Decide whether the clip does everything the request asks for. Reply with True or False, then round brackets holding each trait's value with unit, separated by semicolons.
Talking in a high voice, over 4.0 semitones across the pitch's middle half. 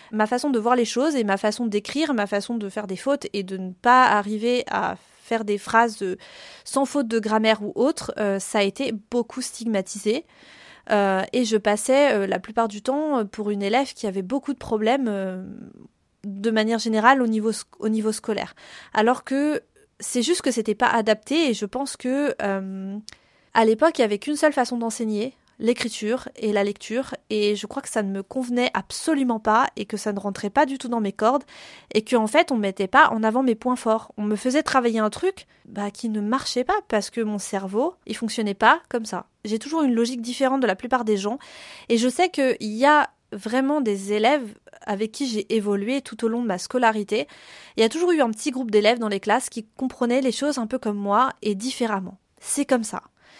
False (230 Hz; 3.6 semitones)